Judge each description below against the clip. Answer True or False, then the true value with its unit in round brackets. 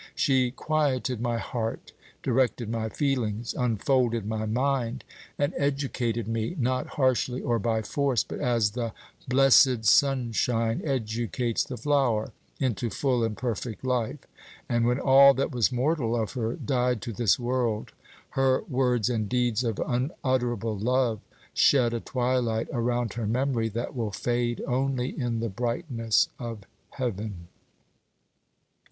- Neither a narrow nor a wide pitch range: False (2.3 semitones)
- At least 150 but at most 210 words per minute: False (135 wpm)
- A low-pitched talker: True (120 Hz)